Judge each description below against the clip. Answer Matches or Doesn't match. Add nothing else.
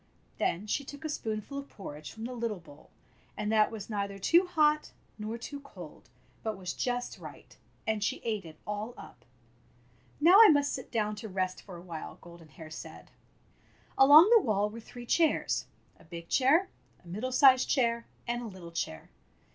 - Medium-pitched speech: Doesn't match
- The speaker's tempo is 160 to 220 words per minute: Matches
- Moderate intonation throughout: Doesn't match